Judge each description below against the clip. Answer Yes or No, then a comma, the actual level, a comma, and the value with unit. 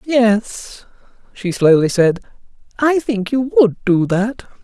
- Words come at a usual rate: No, slow, 130 wpm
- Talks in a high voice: Yes, high, 220 Hz